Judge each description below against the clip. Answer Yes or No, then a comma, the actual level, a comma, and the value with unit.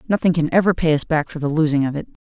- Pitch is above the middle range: No, medium, 160 Hz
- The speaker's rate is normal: No, fast, 290 wpm